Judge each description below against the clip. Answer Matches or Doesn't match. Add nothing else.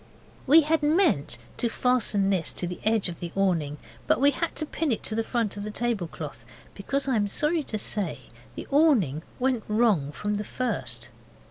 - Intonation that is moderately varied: Doesn't match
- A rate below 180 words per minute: Doesn't match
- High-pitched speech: Matches